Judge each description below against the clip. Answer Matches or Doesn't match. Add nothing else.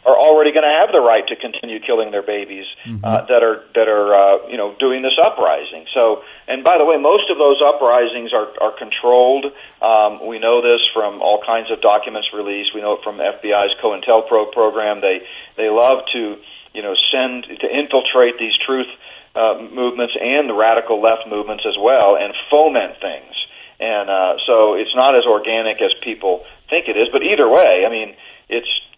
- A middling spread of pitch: Matches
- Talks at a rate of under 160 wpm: Doesn't match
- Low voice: Matches